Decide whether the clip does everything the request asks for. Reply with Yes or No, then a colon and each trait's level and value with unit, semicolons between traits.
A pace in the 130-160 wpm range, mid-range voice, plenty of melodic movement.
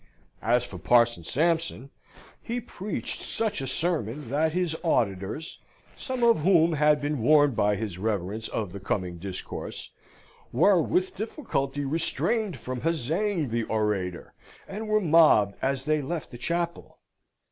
Yes: average, 140 wpm; medium, 145 Hz; wide, 7.3 semitones